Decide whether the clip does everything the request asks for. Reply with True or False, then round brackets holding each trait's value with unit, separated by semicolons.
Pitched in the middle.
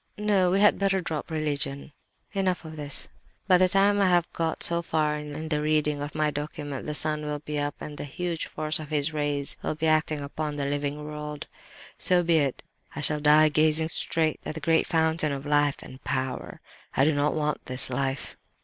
True (150 Hz)